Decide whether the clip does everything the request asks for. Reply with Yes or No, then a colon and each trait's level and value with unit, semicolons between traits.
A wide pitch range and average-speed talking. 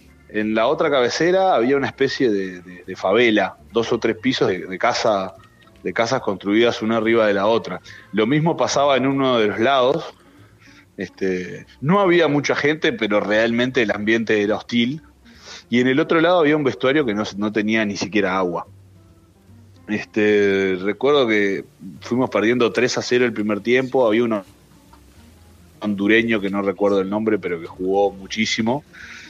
No: average, 3.9 semitones; average, 170 wpm